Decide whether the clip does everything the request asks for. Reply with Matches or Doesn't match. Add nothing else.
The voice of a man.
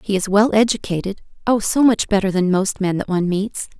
Doesn't match